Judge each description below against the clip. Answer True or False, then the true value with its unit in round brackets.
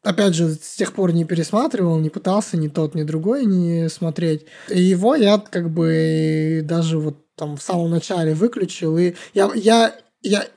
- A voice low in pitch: False (170 Hz)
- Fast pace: True (175 wpm)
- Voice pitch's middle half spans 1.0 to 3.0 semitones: False (3.8 semitones)